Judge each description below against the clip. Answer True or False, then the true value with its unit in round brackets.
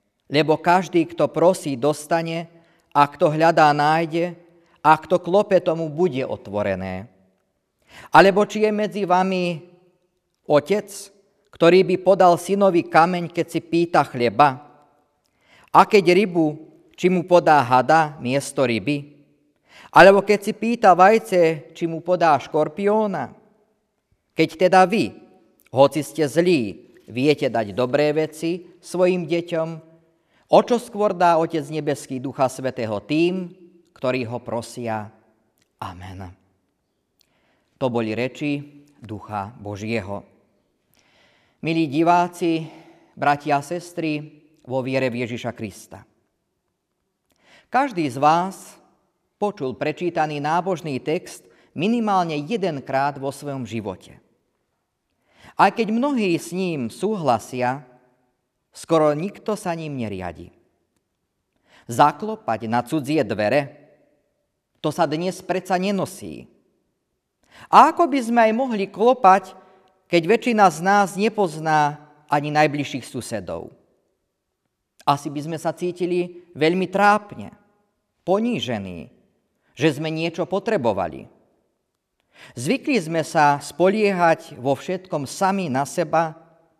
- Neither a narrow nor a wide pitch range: True (4.8 semitones)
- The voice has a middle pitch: True (160 Hz)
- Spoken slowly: True (105 wpm)